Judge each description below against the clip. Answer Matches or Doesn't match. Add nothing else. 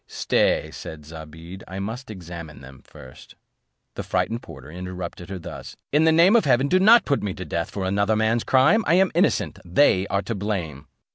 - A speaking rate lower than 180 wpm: Doesn't match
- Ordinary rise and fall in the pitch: Doesn't match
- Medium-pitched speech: Doesn't match